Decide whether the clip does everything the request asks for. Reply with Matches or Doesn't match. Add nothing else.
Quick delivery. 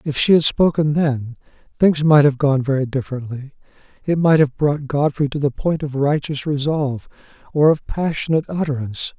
Doesn't match